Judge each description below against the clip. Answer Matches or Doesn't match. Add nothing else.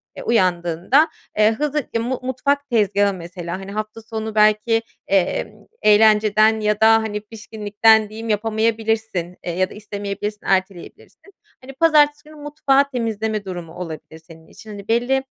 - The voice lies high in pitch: Matches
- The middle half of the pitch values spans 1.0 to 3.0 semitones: Matches